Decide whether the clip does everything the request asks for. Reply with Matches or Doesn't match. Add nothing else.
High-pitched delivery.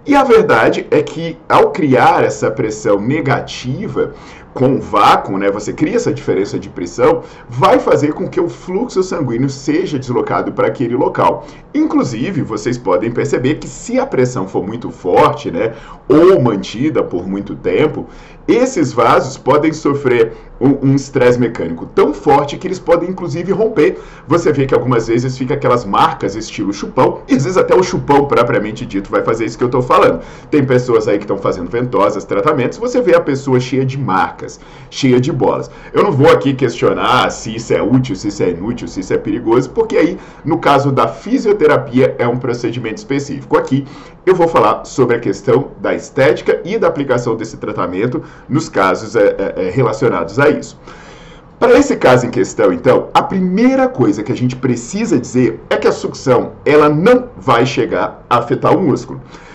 Doesn't match